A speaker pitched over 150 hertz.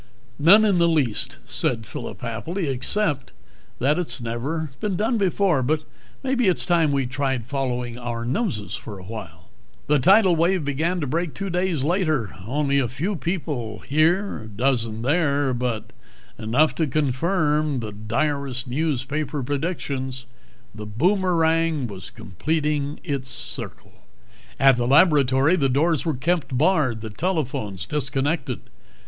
No: medium, 145 Hz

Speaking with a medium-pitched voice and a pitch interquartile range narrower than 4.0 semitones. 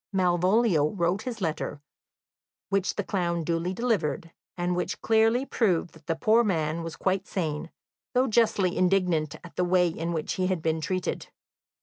Yes: medium, 180 Hz; average, 3.0 semitones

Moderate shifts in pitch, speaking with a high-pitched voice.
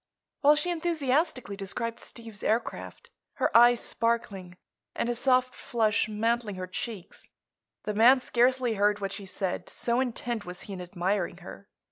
Yes: average, 3.7 semitones; high, 230 Hz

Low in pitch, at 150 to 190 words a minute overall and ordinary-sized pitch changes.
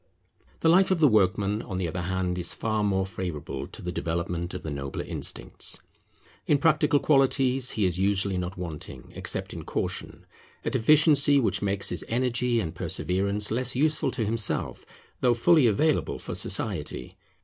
No: low, 105 Hz; average, 165 wpm; wide, 6.4 semitones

